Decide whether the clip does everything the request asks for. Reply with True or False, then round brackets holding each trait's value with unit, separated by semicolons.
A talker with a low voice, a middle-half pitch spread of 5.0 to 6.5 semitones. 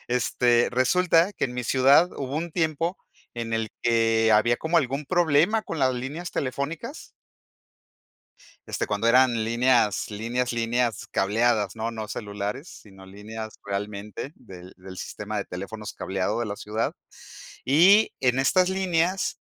True (120 Hz; 5.6 semitones)